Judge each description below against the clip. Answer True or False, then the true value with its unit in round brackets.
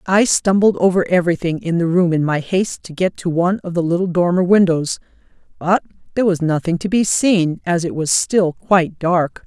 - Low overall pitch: False (175 Hz)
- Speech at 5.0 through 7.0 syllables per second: True (5.4 syllables/s)